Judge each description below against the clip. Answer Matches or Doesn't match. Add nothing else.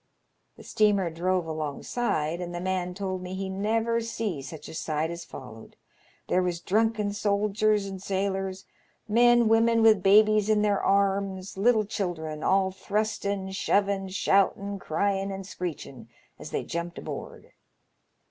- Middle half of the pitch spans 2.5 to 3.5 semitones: Matches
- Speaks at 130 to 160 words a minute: Matches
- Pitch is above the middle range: Matches